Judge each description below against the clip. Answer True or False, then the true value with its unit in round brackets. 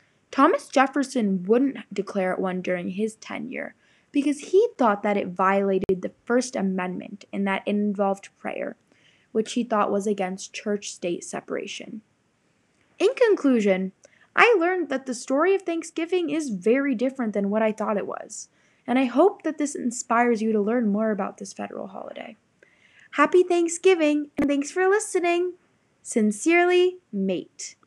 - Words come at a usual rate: True (155 wpm)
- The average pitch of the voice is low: False (245 Hz)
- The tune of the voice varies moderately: False (8.1 semitones)